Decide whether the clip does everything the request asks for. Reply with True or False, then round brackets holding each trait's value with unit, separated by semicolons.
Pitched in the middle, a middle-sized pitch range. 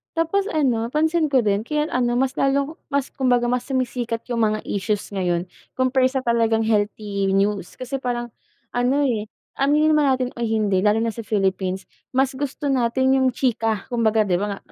False (240 Hz; 4.0 semitones)